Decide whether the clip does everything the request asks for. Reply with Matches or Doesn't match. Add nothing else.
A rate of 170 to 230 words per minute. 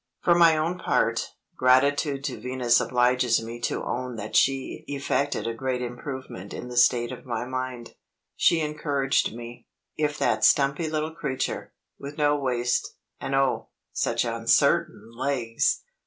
Doesn't match